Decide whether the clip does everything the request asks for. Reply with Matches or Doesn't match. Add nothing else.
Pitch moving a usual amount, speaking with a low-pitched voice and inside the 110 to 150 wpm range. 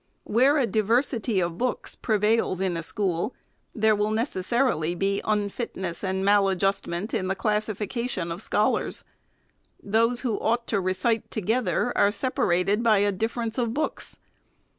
Doesn't match